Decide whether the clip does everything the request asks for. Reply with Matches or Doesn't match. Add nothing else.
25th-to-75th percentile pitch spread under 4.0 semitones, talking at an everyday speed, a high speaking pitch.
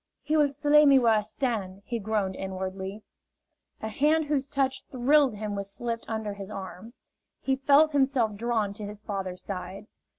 Doesn't match